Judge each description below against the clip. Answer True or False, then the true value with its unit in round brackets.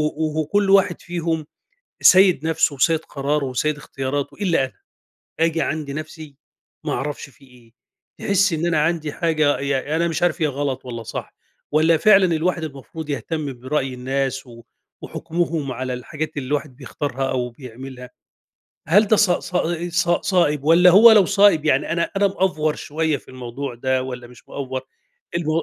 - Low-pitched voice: False (150 Hz)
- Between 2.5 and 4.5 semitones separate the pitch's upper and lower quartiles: True (4.0 semitones)